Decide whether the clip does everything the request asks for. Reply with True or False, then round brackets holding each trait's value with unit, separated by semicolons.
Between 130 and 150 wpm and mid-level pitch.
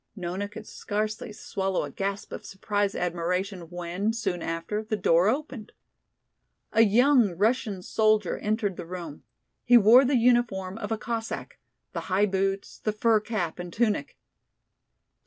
False (145 wpm; 205 Hz)